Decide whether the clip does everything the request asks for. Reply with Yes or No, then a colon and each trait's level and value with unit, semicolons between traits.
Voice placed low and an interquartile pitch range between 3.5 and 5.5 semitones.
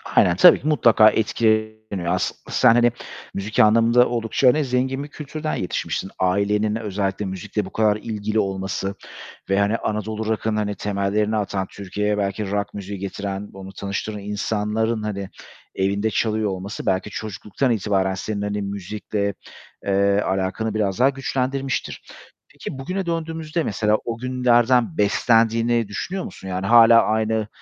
No: low, 105 Hz; narrow, 2.6 semitones